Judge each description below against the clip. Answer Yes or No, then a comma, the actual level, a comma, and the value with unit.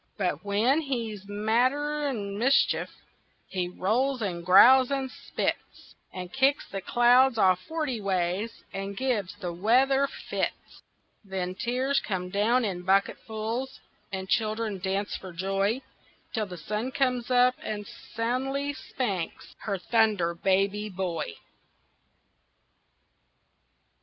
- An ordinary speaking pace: No, slow, 115 wpm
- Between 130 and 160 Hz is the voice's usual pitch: No, high, 215 Hz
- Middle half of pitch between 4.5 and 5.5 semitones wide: Yes, average, 4.9 semitones